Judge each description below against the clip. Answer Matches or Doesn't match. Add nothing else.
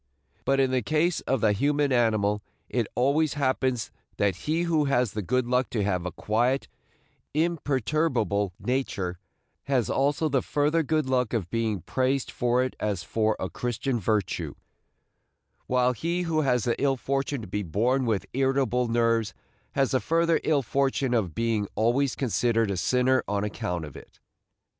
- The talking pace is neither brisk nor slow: Matches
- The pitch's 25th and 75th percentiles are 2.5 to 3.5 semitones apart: Doesn't match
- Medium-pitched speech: Doesn't match